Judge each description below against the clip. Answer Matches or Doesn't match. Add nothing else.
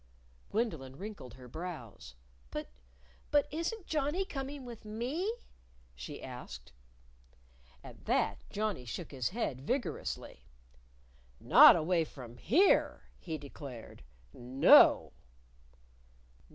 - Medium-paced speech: Doesn't match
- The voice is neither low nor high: Matches